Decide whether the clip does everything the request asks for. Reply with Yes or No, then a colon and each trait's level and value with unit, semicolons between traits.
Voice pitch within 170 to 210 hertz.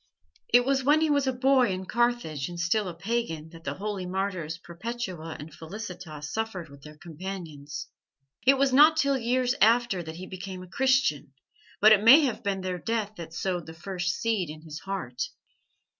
Yes: high, 190 Hz